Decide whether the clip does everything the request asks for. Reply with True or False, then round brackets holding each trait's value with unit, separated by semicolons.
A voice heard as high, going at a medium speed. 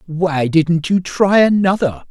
False (175 Hz; 145 wpm)